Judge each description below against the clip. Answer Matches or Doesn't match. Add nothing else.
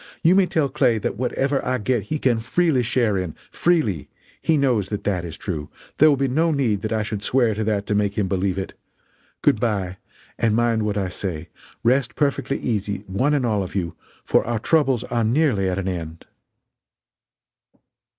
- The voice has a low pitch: Matches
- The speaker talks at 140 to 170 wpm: Doesn't match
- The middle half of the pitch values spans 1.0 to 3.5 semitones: Doesn't match